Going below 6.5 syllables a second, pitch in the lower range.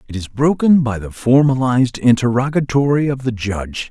Yes: 5.4 syllables/s; low, 125 Hz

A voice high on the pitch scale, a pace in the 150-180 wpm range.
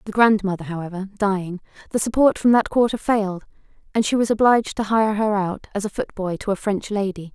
No: high, 205 Hz; fast, 205 wpm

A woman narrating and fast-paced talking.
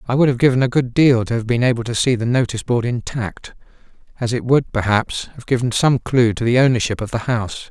No: male; fast, 240 wpm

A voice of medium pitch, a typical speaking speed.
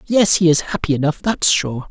No: medium, 165 Hz; fast, 220 wpm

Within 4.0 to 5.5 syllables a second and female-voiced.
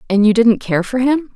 Yes: 5.1 syllables/s; female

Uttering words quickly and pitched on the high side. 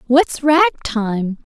No: slow, 115 wpm; high, 240 Hz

